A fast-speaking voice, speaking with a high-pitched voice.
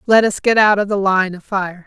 Yes: fast, 290 wpm; high, 200 Hz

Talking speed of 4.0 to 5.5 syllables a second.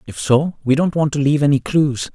No: 5.7 syllables/s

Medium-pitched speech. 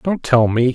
No: low, 130 Hz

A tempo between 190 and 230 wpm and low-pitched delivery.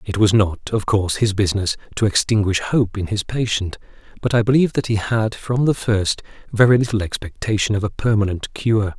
Yes: average, 195 wpm; low, 105 Hz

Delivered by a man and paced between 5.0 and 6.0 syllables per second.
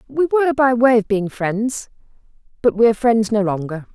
No: female; 5.3 syllables/s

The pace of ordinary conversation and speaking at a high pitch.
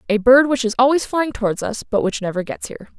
No: fast, 260 wpm; high, 240 Hz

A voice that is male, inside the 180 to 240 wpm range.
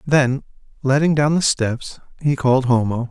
No: male; average, 155 wpm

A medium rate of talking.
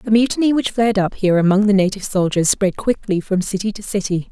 No: fast, 220 wpm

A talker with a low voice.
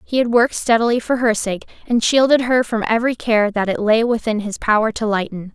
No: high, 225 Hz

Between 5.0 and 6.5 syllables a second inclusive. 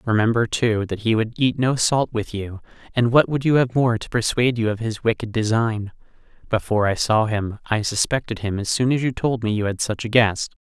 Yes: 5.4 syllables/s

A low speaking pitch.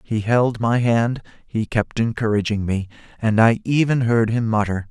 Yes: low, 115 Hz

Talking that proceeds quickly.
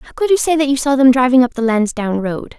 Yes: fast, 300 wpm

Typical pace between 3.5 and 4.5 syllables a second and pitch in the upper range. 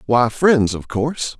No: 4.0 syllables/s; low, 130 Hz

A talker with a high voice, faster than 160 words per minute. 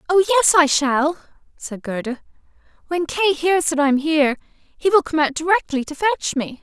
Yes: very high, 310 Hz; average, 190 wpm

